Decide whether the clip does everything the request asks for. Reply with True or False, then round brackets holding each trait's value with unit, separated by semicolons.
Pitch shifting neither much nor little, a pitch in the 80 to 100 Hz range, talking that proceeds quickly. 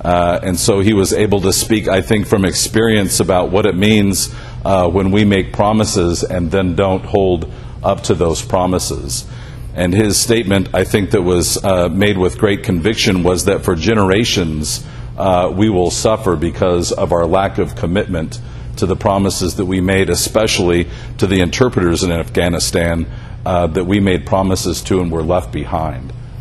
False (3.4 semitones; 95 Hz; 175 wpm)